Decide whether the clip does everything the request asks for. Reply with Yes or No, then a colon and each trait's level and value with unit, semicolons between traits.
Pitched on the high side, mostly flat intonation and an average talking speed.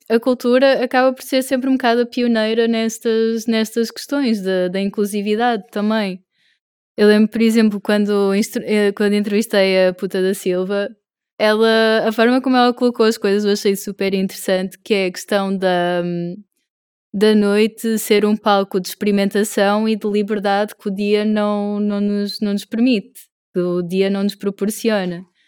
Yes: high, 210 Hz; narrow, 2.1 semitones; average, 165 wpm